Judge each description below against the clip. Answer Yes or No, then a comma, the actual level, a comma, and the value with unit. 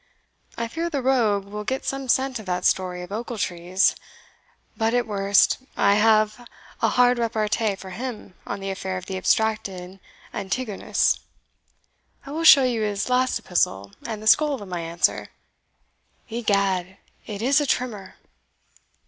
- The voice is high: Yes, high, 215 Hz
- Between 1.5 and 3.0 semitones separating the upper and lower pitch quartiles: No, average, 4.3 semitones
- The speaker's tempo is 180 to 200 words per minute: No, average, 150 wpm